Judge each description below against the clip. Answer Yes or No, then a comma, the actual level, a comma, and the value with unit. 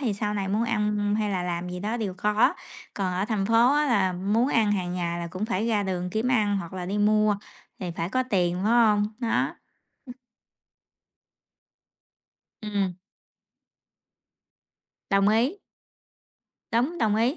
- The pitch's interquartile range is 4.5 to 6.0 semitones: No, average, 3.3 semitones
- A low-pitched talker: No, high, 210 Hz